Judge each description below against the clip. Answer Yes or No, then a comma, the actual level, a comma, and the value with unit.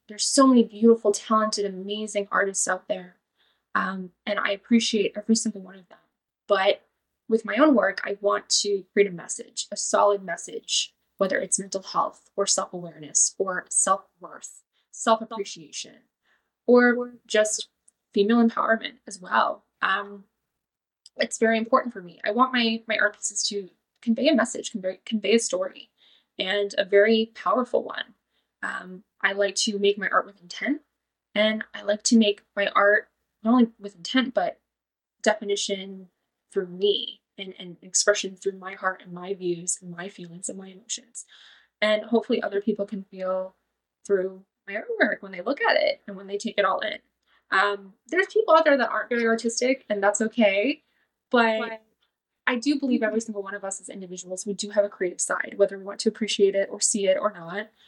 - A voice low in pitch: No, high, 205 Hz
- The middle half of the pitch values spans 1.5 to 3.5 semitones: Yes, average, 2.9 semitones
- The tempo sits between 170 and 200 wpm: Yes, average, 180 wpm